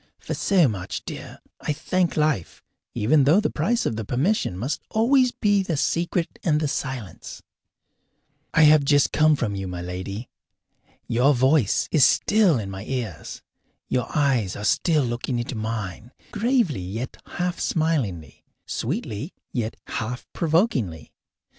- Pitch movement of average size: No, wide, 7.1 semitones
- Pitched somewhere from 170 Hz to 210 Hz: No, low, 135 Hz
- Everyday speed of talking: Yes, average, 145 wpm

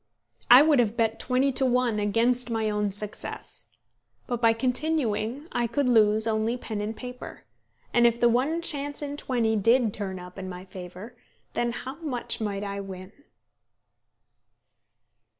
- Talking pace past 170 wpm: No, average, 155 wpm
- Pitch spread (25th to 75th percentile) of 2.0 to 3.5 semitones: Yes, average, 3.2 semitones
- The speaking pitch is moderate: No, high, 230 Hz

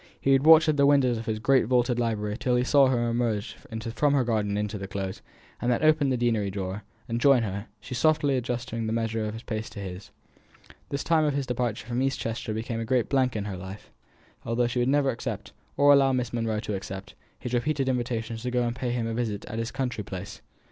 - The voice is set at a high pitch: No, low, 120 Hz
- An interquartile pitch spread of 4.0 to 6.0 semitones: No, average, 3.3 semitones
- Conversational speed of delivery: No, fast, 235 wpm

